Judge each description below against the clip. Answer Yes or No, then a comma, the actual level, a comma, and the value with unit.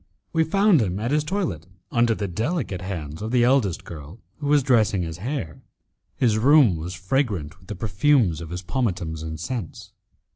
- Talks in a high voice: No, low, 105 Hz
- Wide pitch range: Yes, wide, 7.5 semitones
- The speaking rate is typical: Yes, average, 180 wpm